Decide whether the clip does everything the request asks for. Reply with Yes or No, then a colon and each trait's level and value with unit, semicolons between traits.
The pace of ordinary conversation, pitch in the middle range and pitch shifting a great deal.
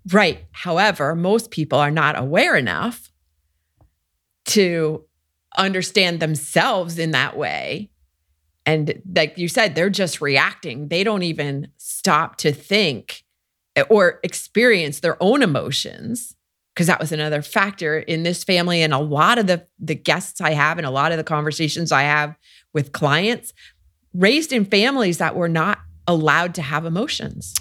No: average, 150 wpm; medium, 160 Hz; average, 4.0 semitones